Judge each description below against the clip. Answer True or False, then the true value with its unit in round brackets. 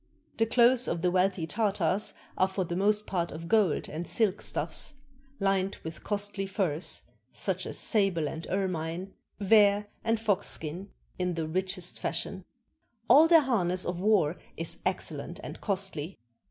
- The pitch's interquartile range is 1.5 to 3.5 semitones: True (3.2 semitones)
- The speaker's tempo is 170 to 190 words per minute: False (155 wpm)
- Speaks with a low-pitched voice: False (190 Hz)